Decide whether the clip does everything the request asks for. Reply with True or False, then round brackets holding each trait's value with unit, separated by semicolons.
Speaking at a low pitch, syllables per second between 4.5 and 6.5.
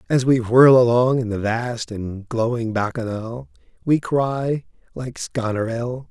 False (115 Hz; 4.0 syllables/s)